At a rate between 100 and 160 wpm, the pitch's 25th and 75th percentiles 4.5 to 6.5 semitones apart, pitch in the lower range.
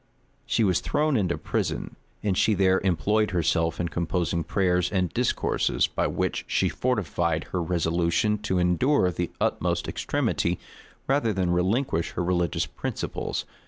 No: average, 140 wpm; average, 3.4 semitones; very low, 90 Hz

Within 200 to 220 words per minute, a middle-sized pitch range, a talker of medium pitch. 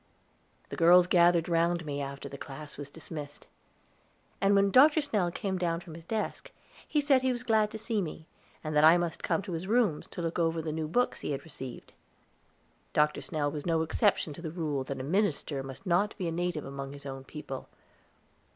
Yes: fast, 205 wpm; average, 4.7 semitones; medium, 165 Hz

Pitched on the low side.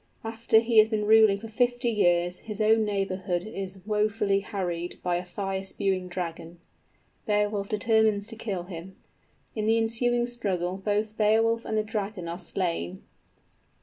No: high, 210 Hz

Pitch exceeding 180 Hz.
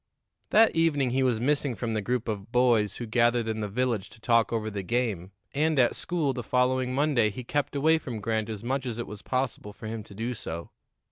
No: low, 120 Hz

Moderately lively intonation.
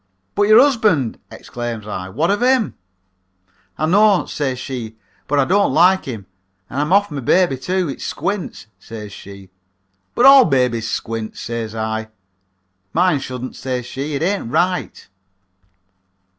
No: wide, 8.4 semitones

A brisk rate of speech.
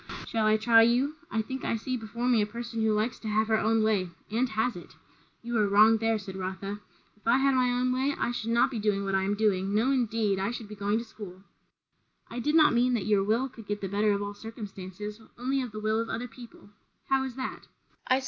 Yes: fast, 235 wpm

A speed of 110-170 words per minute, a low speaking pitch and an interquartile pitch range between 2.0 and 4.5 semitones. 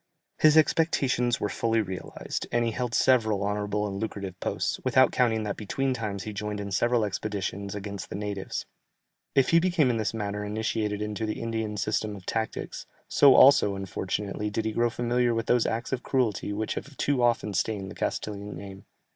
No: average, 185 wpm; low, 110 Hz; average, 2.9 semitones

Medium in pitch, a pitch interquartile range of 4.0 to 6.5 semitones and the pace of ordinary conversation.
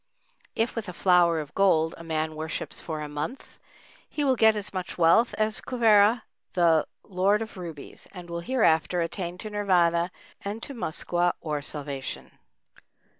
Yes: medium, 180 Hz; average, 4.7 semitones; average, 160 wpm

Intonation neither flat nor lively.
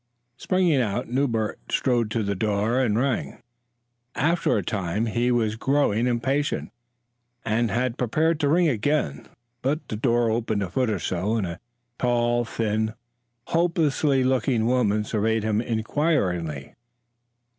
Yes: average, 3.8 semitones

